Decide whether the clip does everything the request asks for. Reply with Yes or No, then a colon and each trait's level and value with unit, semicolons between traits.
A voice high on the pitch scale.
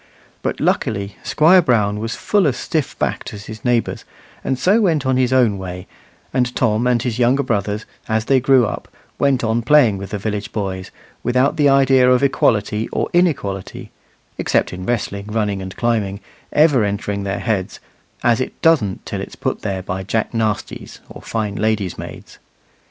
No: low, 115 Hz